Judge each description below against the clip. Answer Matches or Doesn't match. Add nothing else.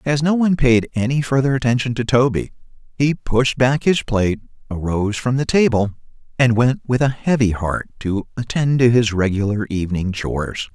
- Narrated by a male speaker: Matches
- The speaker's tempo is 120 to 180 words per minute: Matches